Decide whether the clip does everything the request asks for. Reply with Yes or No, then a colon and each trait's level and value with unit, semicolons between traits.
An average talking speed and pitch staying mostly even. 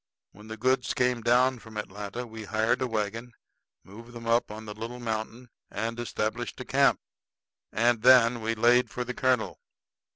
Yes: average, 165 wpm; narrow, 2.0 semitones